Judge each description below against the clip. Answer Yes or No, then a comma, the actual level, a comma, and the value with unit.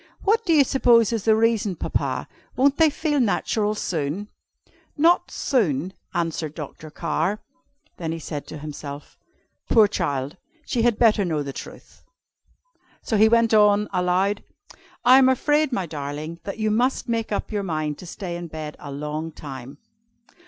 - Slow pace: No, average, 160 wpm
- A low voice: No, high, 195 Hz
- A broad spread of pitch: Yes, wide, 6.9 semitones